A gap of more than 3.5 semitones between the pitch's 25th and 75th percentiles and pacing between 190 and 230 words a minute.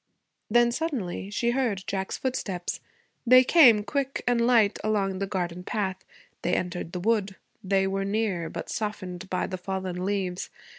No: average, 3.9 semitones; average, 155 wpm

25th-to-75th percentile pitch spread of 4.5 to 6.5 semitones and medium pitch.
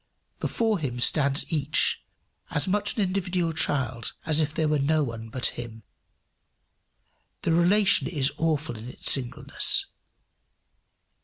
Yes: average, 4.9 semitones; medium, 150 Hz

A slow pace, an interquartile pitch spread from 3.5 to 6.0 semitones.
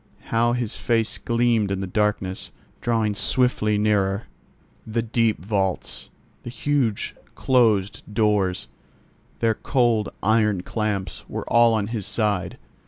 No: slow, 120 wpm; narrow, 2.5 semitones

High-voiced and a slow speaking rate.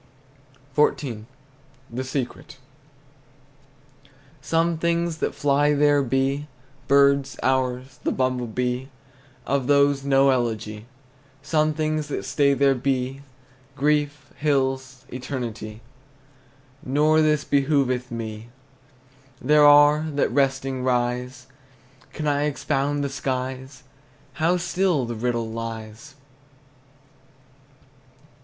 No: low, 135 Hz; slow, 95 wpm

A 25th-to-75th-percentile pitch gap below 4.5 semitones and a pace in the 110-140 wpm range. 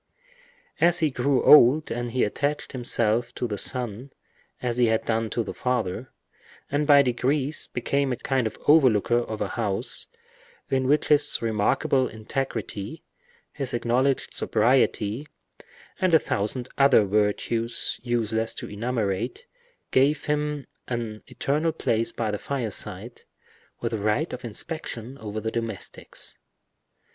Yes: average, 3.8 semitones; slow, 135 wpm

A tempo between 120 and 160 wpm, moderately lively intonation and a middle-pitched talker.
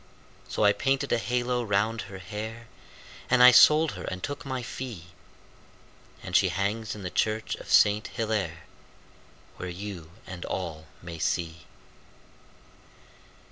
No: average, 140 wpm; average, 4.8 semitones; low, 105 Hz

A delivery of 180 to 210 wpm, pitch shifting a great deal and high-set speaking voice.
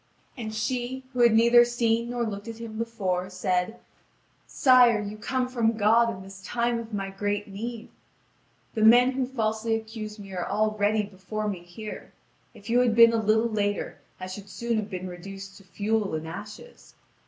No: average, 185 wpm; average, 2.7 semitones; high, 220 Hz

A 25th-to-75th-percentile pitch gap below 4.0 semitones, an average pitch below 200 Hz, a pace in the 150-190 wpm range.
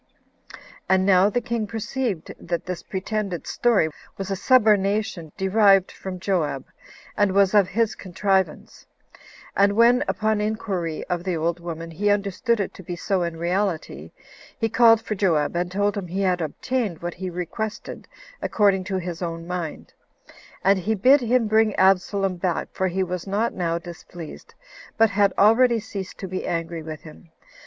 Yes: average, 3.3 semitones; high, 190 Hz; average, 165 wpm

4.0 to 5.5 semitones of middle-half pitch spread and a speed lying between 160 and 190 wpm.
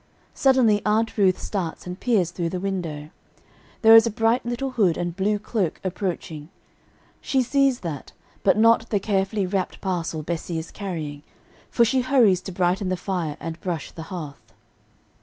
Yes: average, 4.6 semitones; average, 165 wpm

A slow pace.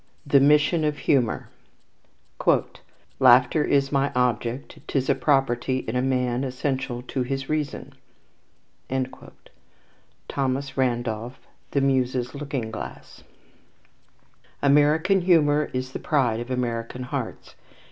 Yes: slow, 105 wpm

